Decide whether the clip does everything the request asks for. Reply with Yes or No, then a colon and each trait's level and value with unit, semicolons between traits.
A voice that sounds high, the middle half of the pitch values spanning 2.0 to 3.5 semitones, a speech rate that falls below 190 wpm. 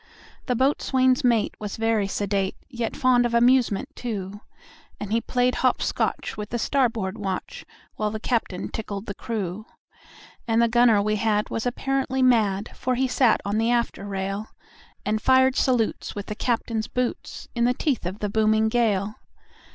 Yes: high, 225 Hz; average, 3.0 semitones; average, 165 wpm